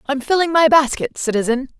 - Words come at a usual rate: Yes, average, 170 wpm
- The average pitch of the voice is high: Yes, very high, 280 Hz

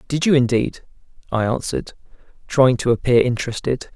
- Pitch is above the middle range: No, low, 125 Hz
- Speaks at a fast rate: No, slow, 135 wpm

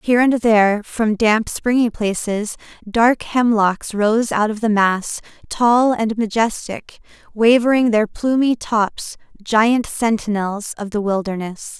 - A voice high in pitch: Yes, high, 220 Hz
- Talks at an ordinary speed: No, slow, 130 wpm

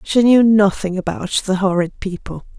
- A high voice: Yes, high, 200 Hz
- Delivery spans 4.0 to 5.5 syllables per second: Yes, 4.7 syllables/s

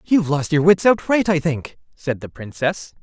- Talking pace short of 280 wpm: Yes, average, 200 wpm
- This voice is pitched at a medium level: Yes, medium, 165 Hz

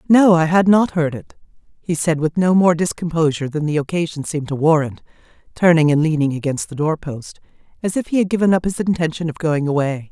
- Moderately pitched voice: Yes, medium, 165 Hz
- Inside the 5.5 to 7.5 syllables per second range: Yes, 5.9 syllables/s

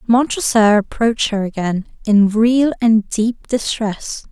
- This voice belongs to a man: No, female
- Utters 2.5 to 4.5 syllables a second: Yes, 3.9 syllables/s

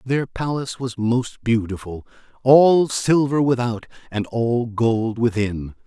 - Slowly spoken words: Yes, slow, 125 wpm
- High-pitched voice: No, low, 120 Hz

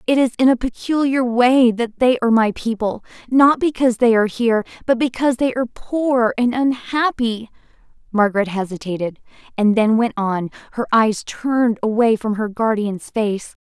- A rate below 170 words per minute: Yes, average, 160 wpm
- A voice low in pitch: No, high, 235 Hz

